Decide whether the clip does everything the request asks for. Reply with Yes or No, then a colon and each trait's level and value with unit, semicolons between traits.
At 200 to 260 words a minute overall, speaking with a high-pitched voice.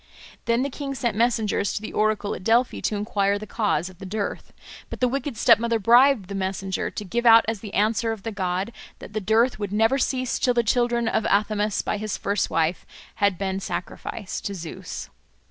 Yes: fast, 205 wpm; high, 215 Hz